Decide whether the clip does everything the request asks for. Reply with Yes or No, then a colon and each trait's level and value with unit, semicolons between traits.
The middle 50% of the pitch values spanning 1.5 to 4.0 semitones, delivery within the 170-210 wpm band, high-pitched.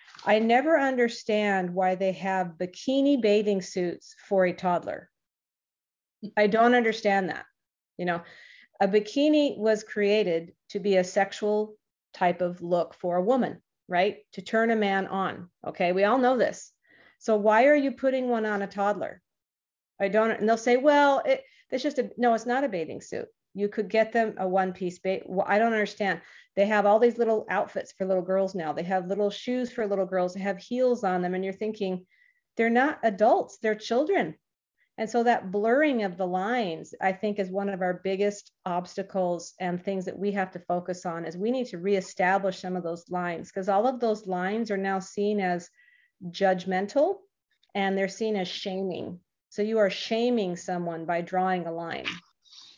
Yes: average, 3.5 semitones; average, 190 wpm; high, 200 Hz